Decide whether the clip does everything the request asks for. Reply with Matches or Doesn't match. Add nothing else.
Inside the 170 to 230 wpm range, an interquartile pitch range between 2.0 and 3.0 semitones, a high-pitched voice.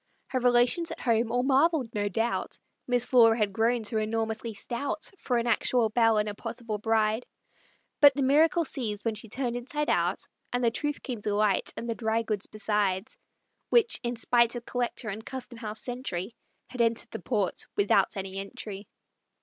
Matches